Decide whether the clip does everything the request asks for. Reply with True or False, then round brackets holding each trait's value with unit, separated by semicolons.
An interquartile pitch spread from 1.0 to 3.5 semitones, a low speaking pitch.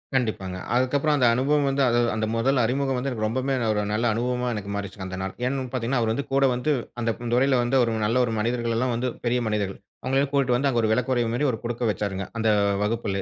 True (3.1 semitones; 120 Hz)